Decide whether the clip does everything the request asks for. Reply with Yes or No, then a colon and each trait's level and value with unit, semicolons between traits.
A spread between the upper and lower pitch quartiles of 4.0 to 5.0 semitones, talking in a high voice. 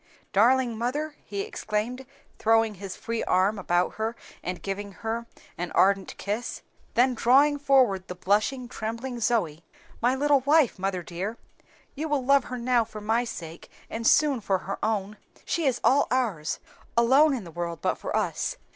Yes: average, 4.7 semitones; high, 225 Hz